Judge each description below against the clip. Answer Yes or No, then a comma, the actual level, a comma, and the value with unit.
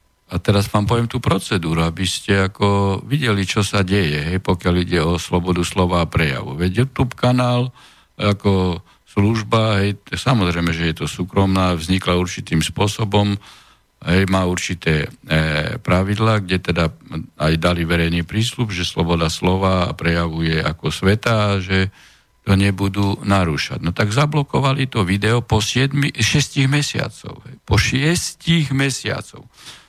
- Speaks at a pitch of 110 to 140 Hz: No, low, 100 Hz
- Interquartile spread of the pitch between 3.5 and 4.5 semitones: Yes, average, 4.2 semitones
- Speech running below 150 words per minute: Yes, average, 140 wpm